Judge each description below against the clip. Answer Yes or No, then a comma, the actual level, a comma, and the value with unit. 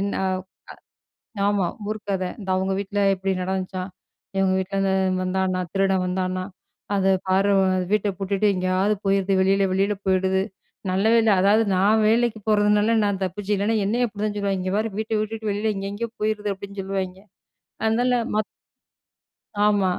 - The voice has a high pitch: Yes, high, 195 Hz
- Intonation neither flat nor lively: No, narrow, 1.8 semitones